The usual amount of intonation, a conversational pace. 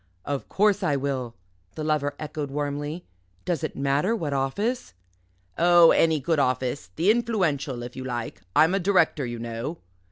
Yes: average, 4.4 semitones; average, 160 wpm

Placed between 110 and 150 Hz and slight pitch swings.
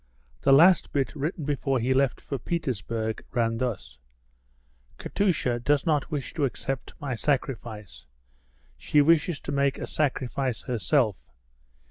No: low, 135 Hz; average, 3.7 semitones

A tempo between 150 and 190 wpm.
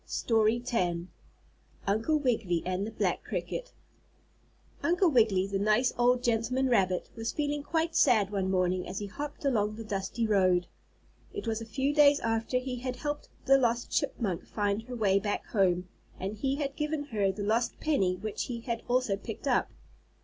Yes: average, 175 wpm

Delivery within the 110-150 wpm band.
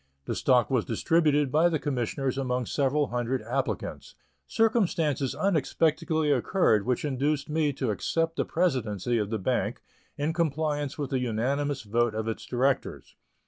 Yes: average, 145 wpm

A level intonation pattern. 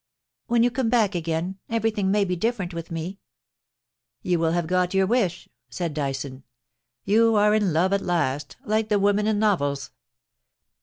No: average, 4.6 semitones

